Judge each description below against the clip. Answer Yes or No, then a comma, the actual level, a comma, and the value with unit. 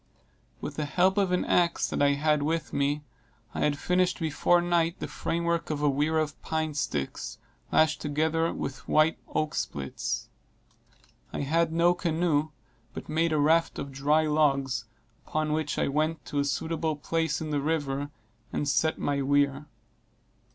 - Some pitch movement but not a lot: No, narrow, 2.3 semitones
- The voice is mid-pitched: Yes, medium, 155 Hz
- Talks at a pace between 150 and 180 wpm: Yes, average, 165 wpm